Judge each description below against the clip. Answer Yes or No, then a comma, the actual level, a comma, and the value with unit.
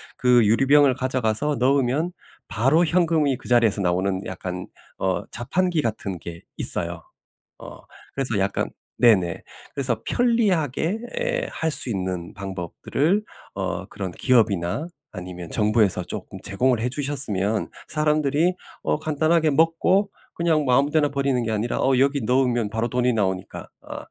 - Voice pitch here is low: Yes, low, 125 Hz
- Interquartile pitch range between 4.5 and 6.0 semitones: No, wide, 6.9 semitones